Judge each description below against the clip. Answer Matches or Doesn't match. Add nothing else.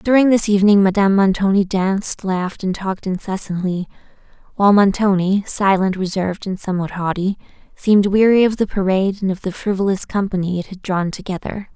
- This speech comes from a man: Doesn't match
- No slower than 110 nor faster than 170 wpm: Matches